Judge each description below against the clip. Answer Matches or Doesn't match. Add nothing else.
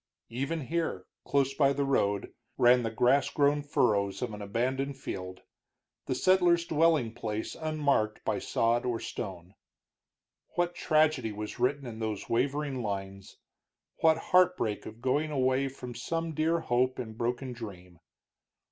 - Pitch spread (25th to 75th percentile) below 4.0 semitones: Doesn't match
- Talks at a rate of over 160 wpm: Doesn't match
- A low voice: Matches